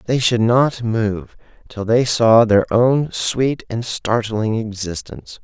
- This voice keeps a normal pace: Yes, average, 145 wpm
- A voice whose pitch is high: No, low, 115 Hz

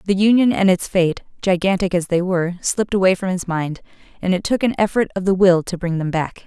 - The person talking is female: Yes, female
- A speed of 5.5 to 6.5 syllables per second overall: Yes, 5.9 syllables/s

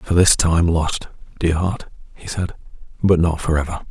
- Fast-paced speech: No, average, 170 wpm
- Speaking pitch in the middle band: No, very low, 85 Hz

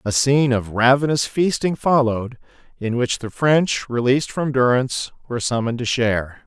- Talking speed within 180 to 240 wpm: No, average, 160 wpm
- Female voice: No, male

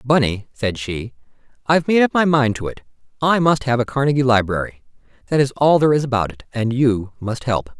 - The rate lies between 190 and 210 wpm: Yes, average, 200 wpm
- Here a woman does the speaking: No, male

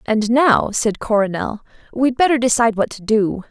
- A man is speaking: No, female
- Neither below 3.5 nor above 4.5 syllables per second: No, 4.9 syllables/s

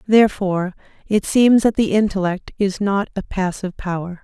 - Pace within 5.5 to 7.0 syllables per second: No, 5.3 syllables/s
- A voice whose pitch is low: No, high, 195 Hz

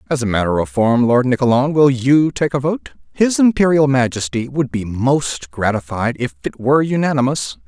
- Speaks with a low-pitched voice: Yes, low, 130 Hz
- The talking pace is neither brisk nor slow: Yes, average, 180 wpm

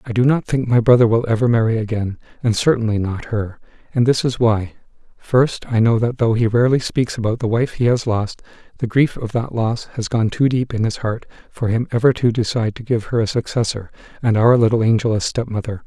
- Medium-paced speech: No, fast, 225 wpm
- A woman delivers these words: No, male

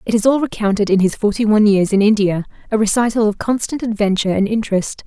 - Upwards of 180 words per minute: Yes, average, 200 wpm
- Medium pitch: No, high, 210 Hz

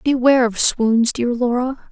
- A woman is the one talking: Yes, female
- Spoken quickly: No, average, 155 wpm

